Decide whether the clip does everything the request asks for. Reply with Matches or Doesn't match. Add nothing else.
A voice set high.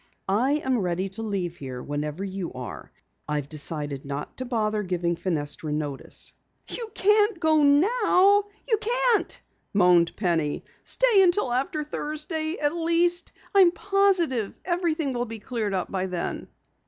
Matches